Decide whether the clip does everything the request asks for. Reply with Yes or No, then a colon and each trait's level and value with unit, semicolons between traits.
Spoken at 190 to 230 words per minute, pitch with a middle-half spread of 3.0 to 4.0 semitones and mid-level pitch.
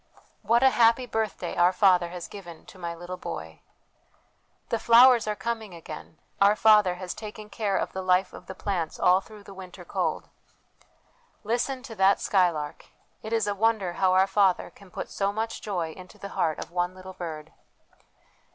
No: average, 195 wpm; average, 3.4 semitones; high, 195 Hz